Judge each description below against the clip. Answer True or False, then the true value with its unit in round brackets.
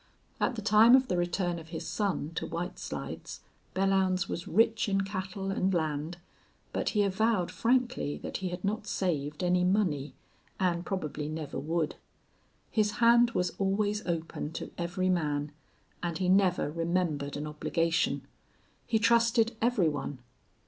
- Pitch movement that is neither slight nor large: True (4.1 semitones)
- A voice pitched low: False (180 Hz)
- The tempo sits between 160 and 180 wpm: False (150 wpm)